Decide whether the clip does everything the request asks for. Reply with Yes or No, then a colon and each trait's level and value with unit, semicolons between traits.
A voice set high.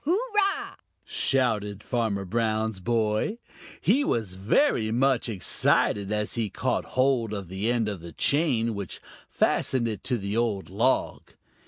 No: low, 110 Hz